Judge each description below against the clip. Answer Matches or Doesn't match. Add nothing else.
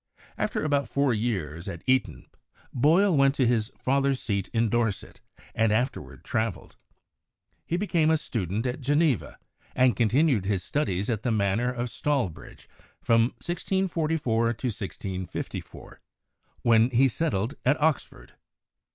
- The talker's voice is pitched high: Doesn't match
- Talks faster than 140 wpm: Doesn't match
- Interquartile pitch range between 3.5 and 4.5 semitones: Doesn't match